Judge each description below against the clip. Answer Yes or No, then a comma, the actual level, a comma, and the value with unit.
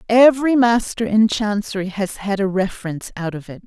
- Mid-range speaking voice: No, high, 210 Hz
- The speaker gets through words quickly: No, average, 180 wpm